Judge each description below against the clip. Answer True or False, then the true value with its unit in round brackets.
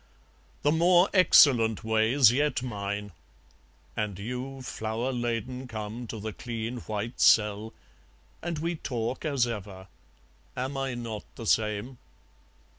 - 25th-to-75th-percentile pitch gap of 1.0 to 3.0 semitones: False (3.5 semitones)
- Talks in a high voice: False (120 Hz)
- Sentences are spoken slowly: True (120 wpm)